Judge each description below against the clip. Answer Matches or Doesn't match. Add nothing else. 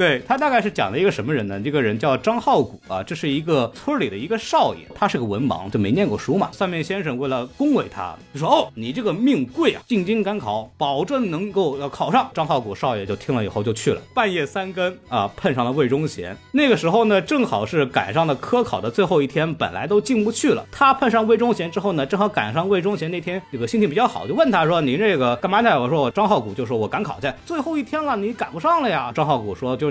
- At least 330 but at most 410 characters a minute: Matches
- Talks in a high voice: Matches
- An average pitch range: Doesn't match